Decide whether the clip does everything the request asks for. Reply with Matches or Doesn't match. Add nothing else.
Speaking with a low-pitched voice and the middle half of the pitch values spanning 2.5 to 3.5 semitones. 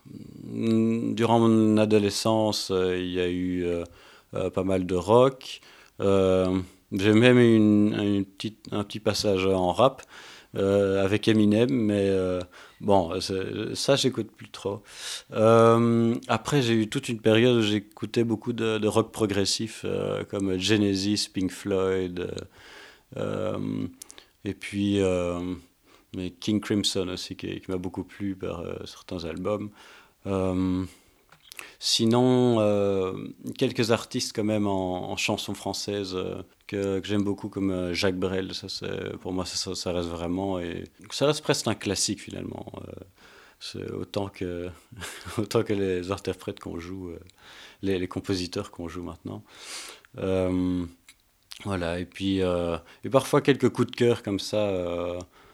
Matches